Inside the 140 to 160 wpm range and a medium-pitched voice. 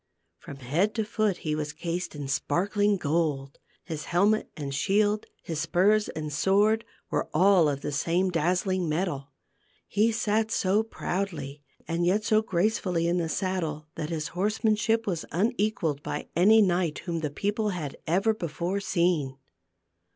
Yes: average, 150 wpm; medium, 180 Hz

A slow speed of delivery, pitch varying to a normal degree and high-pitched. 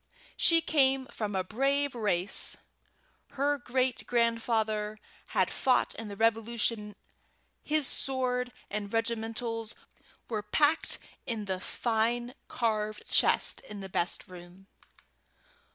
Yes: slow, 110 wpm; average, 3.1 semitones; high, 225 Hz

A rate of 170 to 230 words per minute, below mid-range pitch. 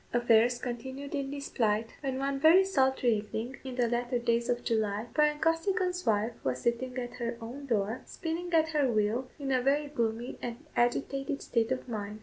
No: average, 185 wpm; very high, 250 Hz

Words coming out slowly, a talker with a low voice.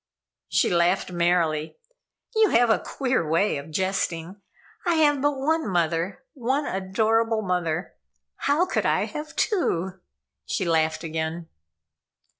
No: slow, 130 wpm; high, 190 Hz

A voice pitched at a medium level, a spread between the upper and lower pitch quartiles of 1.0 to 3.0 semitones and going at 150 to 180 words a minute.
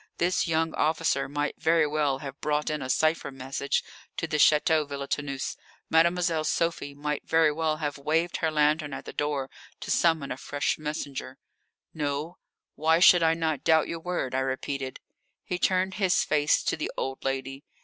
Yes: medium, 150 Hz; narrow, 2.4 semitones; average, 170 wpm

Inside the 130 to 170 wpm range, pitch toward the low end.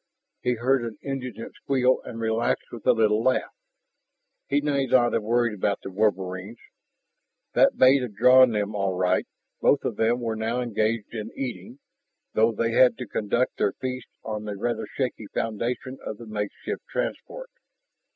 Yes: average, 165 wpm; low, 115 Hz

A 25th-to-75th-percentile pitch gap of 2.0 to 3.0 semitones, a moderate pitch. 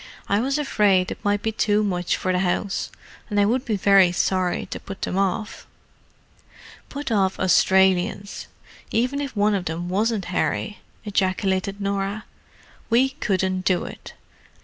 No: narrow, 2.4 semitones; high, 200 Hz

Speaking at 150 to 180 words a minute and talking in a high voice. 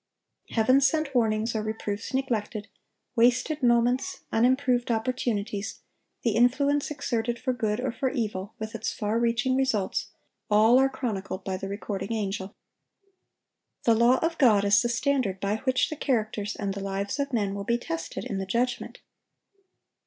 Yes: average, 155 wpm; high, 230 Hz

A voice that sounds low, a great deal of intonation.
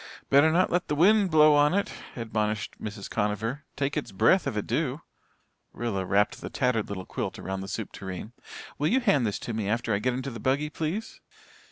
Yes: low, 125 Hz; wide, 6.3 semitones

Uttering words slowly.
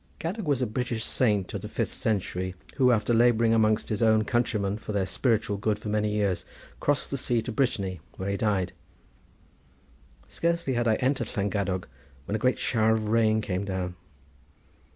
No: average, 175 wpm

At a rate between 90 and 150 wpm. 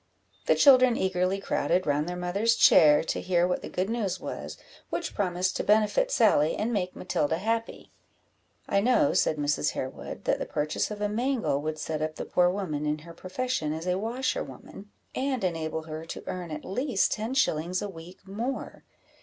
No: average, 185 wpm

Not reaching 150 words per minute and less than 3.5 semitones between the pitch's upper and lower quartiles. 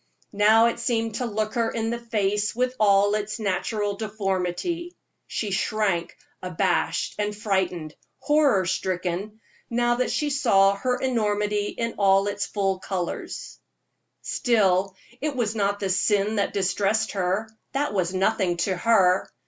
Yes: average, 140 wpm; average, 2.8 semitones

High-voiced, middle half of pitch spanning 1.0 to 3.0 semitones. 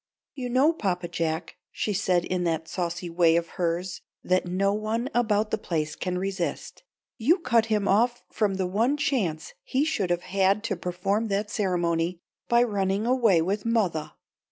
No: high, 195 Hz; average, 4.2 semitones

